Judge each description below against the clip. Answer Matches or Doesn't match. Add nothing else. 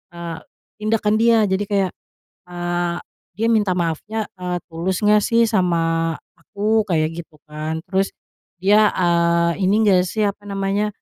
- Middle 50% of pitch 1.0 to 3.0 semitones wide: Doesn't match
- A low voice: Doesn't match